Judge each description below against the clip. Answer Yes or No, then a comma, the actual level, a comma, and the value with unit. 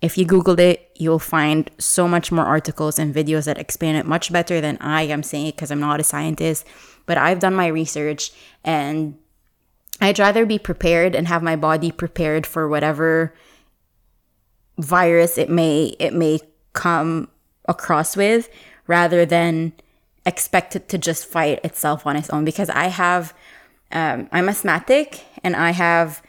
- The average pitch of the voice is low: No, medium, 165 Hz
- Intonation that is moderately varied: No, narrow, 2.3 semitones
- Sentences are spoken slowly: No, average, 165 wpm